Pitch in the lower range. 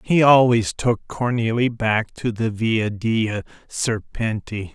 Yes: low, 115 Hz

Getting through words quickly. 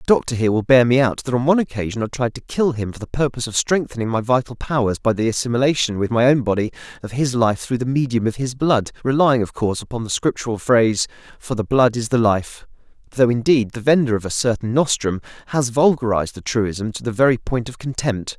Yes: fast, 230 wpm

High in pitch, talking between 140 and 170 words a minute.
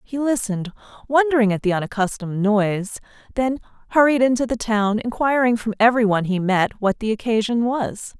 Yes: high, 225 Hz; average, 160 wpm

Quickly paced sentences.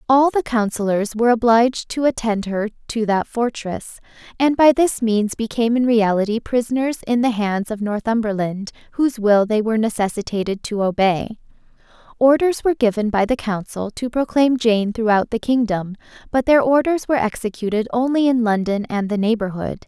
No: average, 165 wpm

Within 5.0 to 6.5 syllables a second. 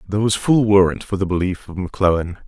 No: 6.9 syllables/s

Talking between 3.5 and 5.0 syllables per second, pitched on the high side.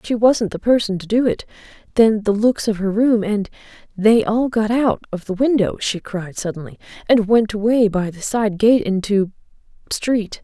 Yes: 4.7 syllables/s; high, 215 Hz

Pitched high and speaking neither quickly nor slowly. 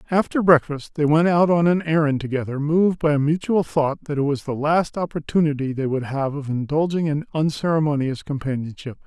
No: medium, 150 Hz; average, 185 wpm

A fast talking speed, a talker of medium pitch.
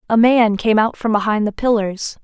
No: fast, 215 wpm; high, 220 Hz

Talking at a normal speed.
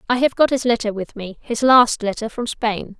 No: fast, 220 wpm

